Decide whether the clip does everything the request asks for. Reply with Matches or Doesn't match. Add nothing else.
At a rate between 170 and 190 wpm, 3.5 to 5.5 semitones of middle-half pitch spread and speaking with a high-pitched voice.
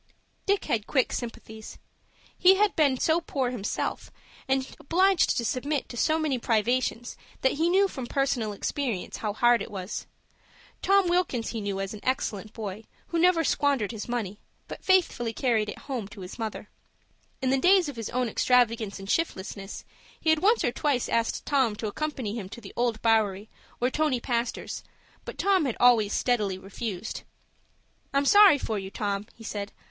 Matches